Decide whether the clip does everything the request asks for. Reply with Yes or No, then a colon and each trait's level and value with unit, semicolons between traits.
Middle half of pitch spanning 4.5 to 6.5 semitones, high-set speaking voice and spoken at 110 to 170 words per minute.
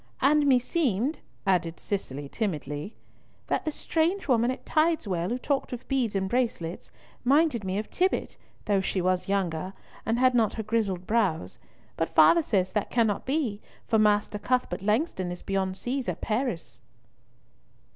Yes: wide, 5.4 semitones; high, 215 Hz; average, 155 wpm